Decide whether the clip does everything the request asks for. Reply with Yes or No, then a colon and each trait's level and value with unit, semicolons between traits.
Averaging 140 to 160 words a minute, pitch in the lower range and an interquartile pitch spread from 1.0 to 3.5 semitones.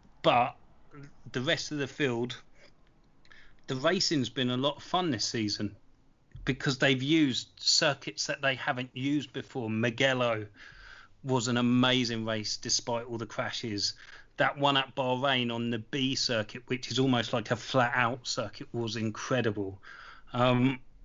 Yes: average, 150 wpm; low, 125 Hz; narrow, 2.6 semitones